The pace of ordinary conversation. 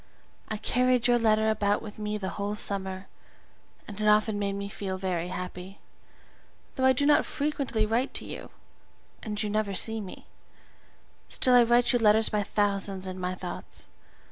Yes: average, 170 wpm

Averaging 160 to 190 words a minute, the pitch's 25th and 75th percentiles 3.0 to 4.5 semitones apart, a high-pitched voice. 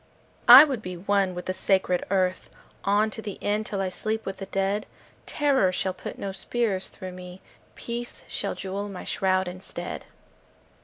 No: average, 170 wpm; narrow, 2.4 semitones; high, 195 Hz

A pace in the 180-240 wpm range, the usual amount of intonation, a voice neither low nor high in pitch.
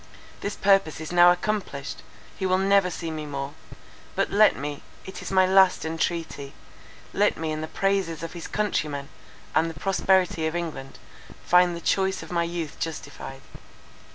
No: average, 165 wpm; average, 3.3 semitones; medium, 170 Hz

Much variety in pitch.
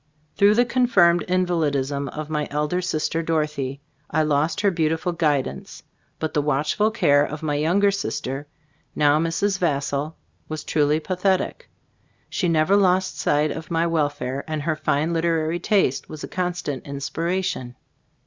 No: average, 3.4 semitones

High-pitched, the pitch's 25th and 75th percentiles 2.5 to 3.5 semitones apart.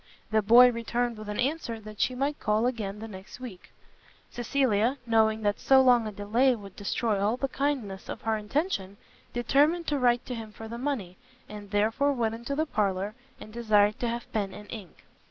Yes: high, 225 Hz; average, 3.2 semitones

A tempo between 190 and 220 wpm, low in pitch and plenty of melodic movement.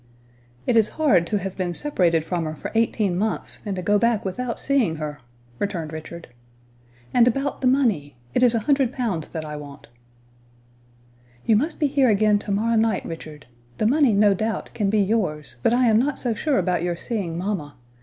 No: average, 195 wpm; high, 210 Hz; wide, 5.7 semitones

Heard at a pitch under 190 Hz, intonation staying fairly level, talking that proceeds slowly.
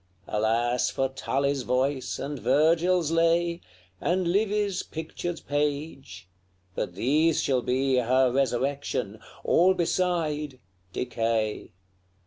No: medium, 140 Hz; average, 4.8 semitones; slow, 100 wpm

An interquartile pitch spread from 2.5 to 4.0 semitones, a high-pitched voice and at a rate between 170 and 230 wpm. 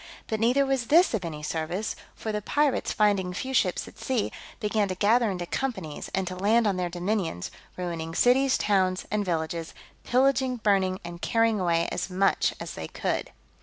No: average, 4.7 semitones; high, 200 Hz; average, 180 wpm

